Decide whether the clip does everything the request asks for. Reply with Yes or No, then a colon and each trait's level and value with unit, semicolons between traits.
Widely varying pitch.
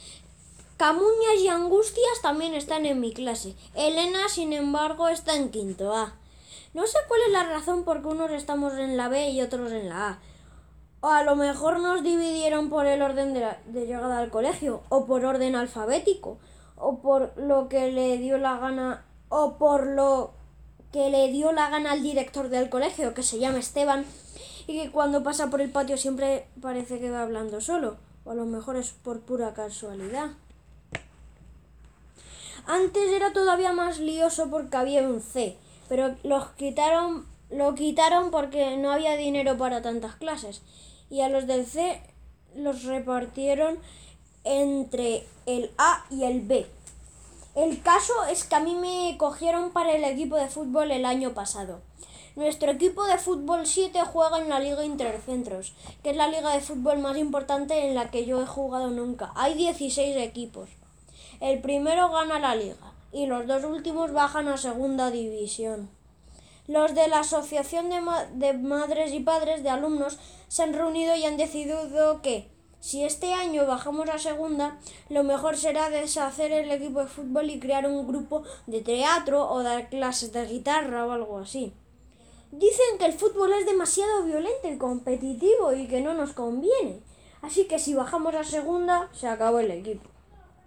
No: average, 3.6 semitones